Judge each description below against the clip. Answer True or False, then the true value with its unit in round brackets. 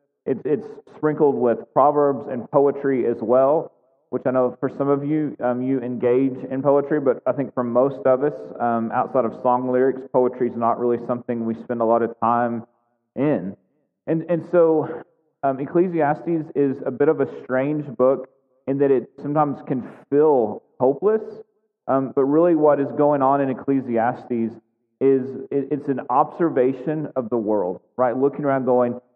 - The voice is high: False (135 Hz)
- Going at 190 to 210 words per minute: False (175 wpm)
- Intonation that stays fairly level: False (3.1 semitones)